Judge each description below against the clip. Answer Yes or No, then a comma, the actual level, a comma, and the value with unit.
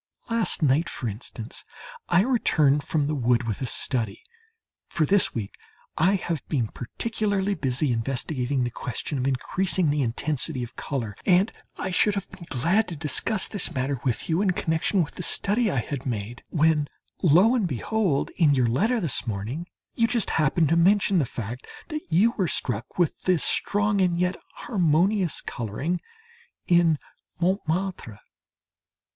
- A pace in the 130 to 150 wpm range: No, average, 160 wpm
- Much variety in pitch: Yes, wide, 6.8 semitones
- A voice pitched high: No, medium, 160 Hz